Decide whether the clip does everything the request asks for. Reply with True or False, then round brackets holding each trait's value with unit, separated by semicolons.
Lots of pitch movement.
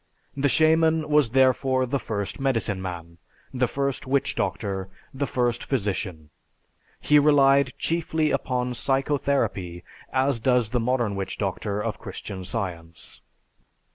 True (5.7 semitones)